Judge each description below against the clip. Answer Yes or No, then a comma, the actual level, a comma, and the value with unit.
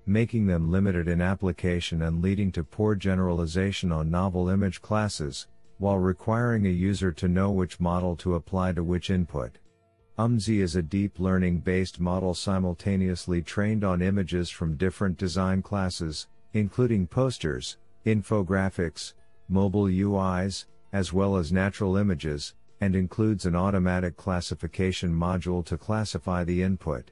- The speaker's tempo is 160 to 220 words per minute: No, slow, 135 wpm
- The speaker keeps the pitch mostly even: Yes, narrow, 2.1 semitones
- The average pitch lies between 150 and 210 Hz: No, very low, 95 Hz